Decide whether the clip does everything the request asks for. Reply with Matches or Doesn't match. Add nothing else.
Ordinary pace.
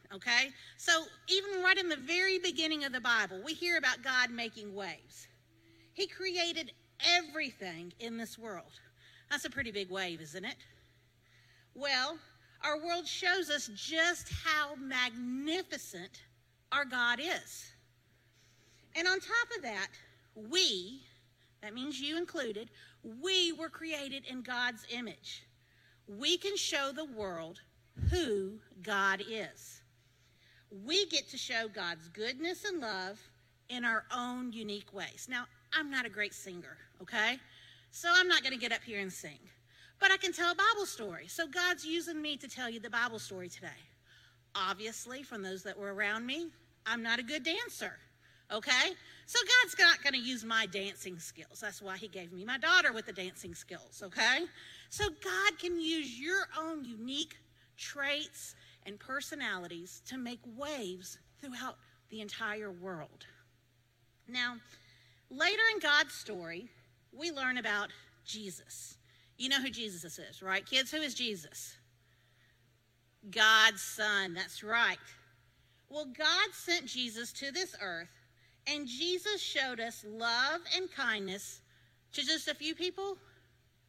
Matches